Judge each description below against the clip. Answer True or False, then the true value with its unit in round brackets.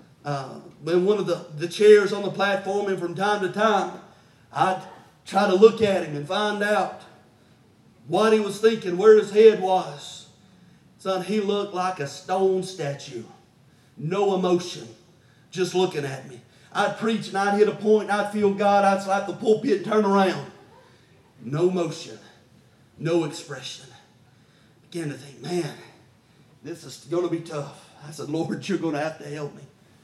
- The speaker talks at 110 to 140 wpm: False (175 wpm)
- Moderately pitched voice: True (180 Hz)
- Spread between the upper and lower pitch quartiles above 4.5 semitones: True (4.9 semitones)